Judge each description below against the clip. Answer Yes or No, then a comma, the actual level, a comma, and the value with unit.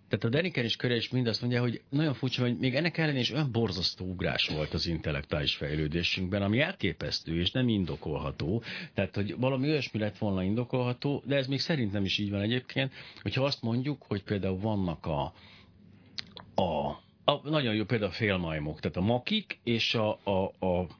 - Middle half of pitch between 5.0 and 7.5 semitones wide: Yes, average, 5.3 semitones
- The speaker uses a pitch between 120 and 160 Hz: No, low, 110 Hz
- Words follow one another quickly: Yes, fast, 180 wpm